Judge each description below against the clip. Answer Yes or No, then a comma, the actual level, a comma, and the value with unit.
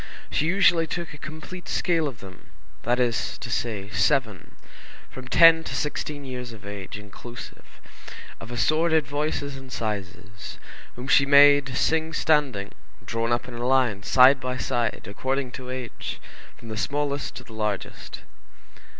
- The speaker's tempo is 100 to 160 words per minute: Yes, average, 150 wpm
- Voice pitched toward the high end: No, low, 130 Hz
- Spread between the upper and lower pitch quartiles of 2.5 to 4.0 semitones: No, average, 4.5 semitones